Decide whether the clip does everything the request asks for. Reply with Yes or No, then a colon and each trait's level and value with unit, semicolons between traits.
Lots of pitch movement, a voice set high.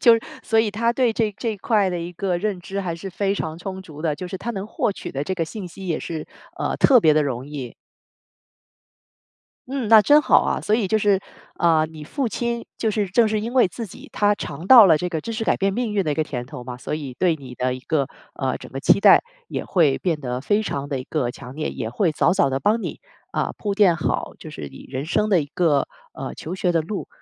No: wide, 5.8 semitones; medium, 180 Hz